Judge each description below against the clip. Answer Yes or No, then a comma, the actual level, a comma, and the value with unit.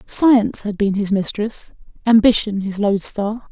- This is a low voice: No, high, 210 Hz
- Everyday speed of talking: Yes, average, 155 wpm